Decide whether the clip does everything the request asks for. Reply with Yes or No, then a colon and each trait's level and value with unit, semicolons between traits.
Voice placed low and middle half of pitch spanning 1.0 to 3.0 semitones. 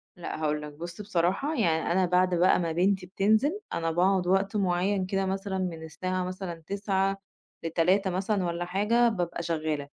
No: medium, 185 Hz; narrow, 2.4 semitones